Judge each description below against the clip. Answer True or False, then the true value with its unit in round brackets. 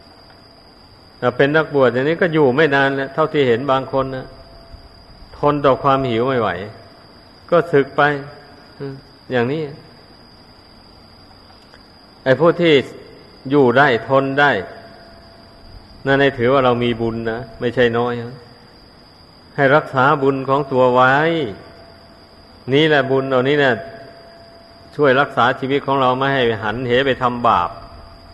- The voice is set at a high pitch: False (130 Hz)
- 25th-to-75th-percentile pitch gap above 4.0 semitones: False (3.7 semitones)